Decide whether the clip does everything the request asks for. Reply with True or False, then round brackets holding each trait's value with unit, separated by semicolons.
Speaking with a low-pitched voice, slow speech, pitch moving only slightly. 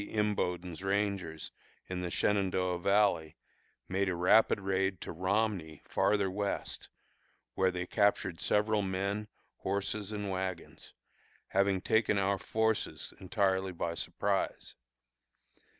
True (95 Hz; 110 wpm; 1.9 semitones)